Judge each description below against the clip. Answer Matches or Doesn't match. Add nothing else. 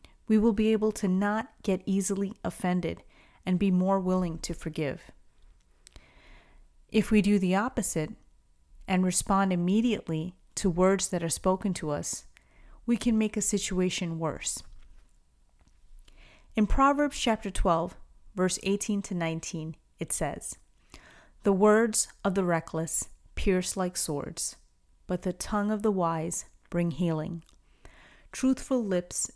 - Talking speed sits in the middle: Doesn't match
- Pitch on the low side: Doesn't match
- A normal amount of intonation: Matches